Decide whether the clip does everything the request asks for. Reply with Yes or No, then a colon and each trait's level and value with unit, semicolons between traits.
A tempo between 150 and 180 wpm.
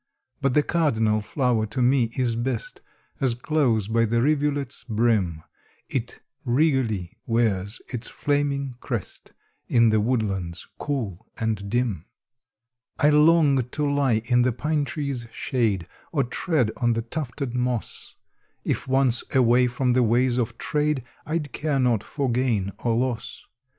No: average, 140 wpm